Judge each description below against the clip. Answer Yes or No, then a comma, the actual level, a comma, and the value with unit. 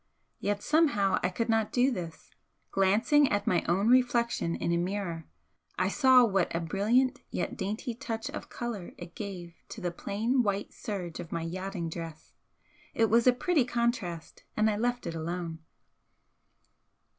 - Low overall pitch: No, high, 205 Hz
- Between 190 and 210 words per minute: No, average, 160 wpm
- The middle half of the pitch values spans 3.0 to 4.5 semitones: No, average, 5.3 semitones